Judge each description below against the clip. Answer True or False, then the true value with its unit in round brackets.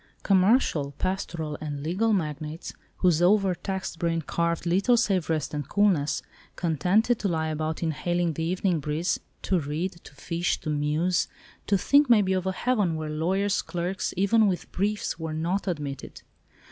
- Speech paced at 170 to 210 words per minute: False (150 wpm)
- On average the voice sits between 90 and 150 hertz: False (175 Hz)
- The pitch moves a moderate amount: True (3.6 semitones)